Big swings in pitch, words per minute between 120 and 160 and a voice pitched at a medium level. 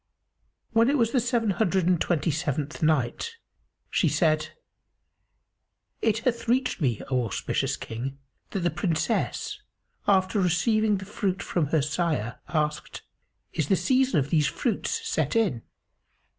Yes: wide, 7.0 semitones; average, 140 wpm; medium, 175 Hz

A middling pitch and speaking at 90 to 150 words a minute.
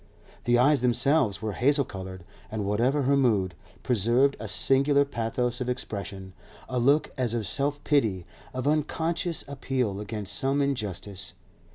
No: low, 125 Hz; average, 145 wpm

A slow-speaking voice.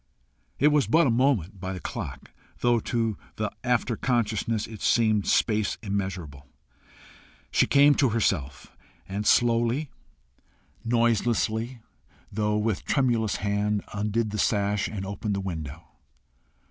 Yes: slow, 125 wpm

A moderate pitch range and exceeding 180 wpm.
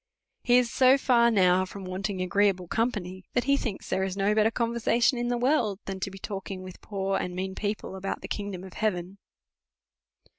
Yes: average, 3.8 semitones; average, 195 wpm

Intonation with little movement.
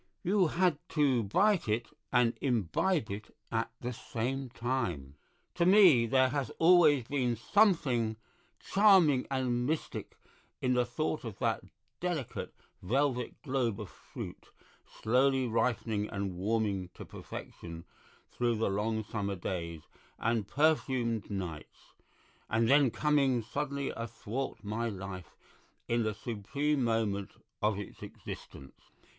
No: average, 4.7 semitones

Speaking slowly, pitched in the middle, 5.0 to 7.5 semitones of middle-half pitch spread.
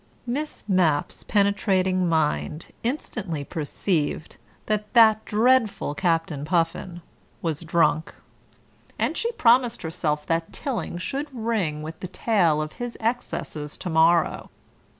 Yes: slow, 115 wpm; medium, 180 Hz; wide, 5.6 semitones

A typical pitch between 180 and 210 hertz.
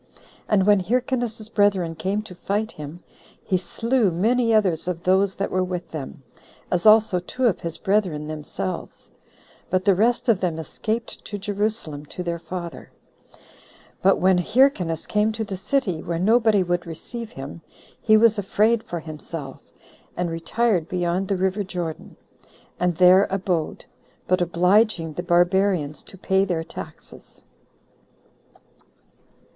Yes: medium, 185 Hz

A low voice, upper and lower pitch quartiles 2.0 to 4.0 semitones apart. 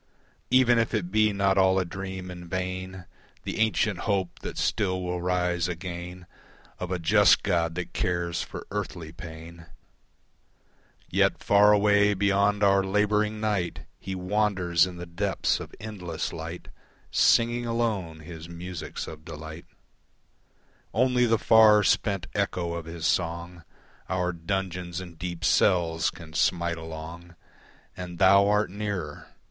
Yes: very low, 90 Hz; average, 3.1 semitones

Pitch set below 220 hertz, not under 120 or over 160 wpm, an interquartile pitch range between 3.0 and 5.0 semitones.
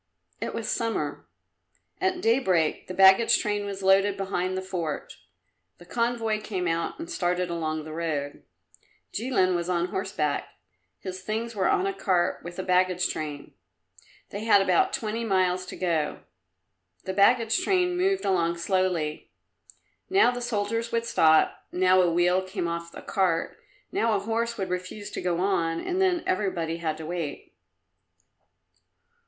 Yes: medium, 185 Hz; average, 155 wpm; average, 4.6 semitones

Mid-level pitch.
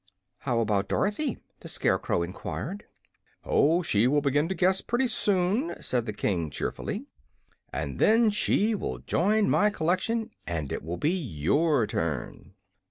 Yes: medium, 155 Hz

